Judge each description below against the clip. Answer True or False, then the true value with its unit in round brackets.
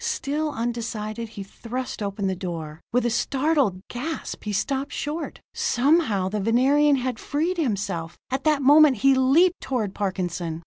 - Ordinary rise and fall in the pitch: False (6.2 semitones)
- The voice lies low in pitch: False (245 Hz)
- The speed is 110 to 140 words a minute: False (150 wpm)